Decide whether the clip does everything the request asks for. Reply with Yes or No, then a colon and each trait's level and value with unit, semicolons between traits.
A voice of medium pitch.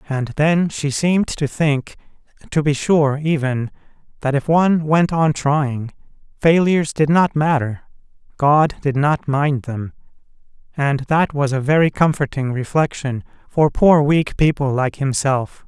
Yes: medium, 145 Hz